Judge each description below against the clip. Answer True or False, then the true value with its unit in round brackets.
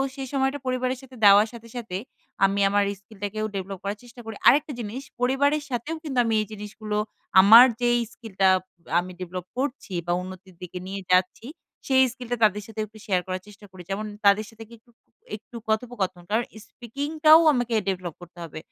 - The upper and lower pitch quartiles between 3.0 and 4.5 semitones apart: True (4.1 semitones)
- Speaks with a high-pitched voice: True (215 Hz)